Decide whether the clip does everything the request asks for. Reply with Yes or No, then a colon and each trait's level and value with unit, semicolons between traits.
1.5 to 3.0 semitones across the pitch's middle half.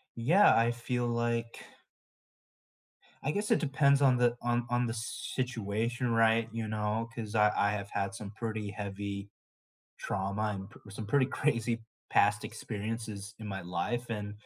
Yes: narrow, 2.6 semitones